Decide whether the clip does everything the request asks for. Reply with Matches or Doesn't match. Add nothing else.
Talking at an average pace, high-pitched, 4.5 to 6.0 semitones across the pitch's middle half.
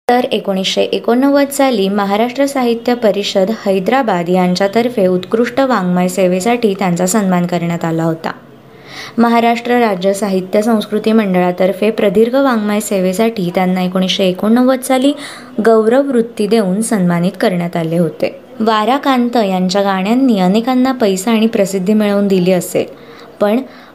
Doesn't match